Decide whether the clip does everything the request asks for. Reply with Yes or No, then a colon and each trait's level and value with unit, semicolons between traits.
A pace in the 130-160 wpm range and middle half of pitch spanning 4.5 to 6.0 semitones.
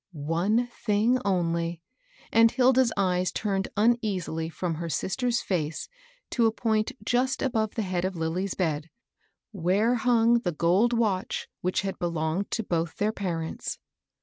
Yes: average, 145 wpm; average, 5.1 semitones